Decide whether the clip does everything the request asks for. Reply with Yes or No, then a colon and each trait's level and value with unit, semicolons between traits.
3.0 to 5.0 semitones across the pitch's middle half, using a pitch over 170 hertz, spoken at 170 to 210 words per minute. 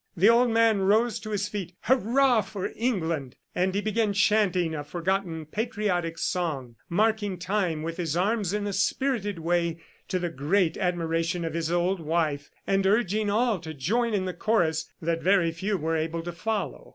Yes: average, 4.2 semitones; medium, 185 Hz; average, 175 wpm